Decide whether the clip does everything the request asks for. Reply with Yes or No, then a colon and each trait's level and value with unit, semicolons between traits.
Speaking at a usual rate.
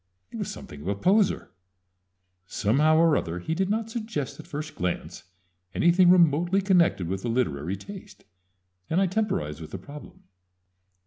Yes: average, 155 wpm